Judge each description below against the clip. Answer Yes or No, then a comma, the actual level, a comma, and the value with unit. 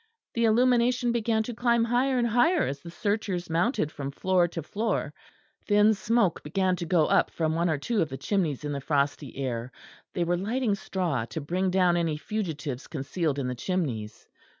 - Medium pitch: Yes, medium, 180 Hz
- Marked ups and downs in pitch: Yes, wide, 6.7 semitones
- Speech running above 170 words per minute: Yes, average, 190 wpm